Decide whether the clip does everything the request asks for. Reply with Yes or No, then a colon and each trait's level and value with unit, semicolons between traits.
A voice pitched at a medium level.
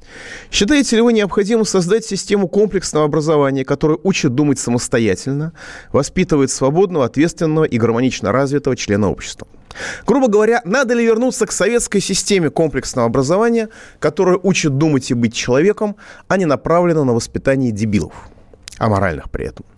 Yes: medium, 160 Hz